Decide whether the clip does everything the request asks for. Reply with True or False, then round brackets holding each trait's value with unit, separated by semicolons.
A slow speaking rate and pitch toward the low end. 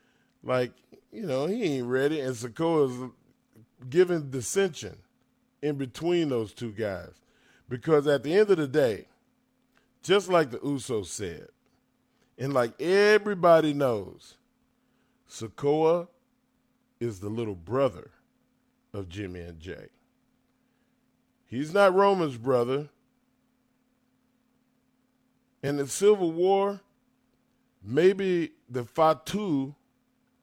False (105 wpm; 170 Hz)